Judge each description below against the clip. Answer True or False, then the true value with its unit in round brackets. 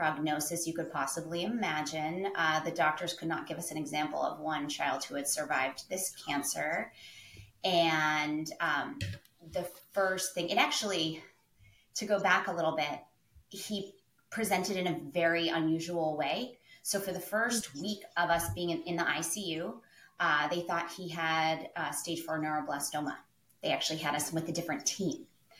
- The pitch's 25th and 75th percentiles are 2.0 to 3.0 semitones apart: True (2.7 semitones)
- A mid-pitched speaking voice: True (165 Hz)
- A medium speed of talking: True (165 wpm)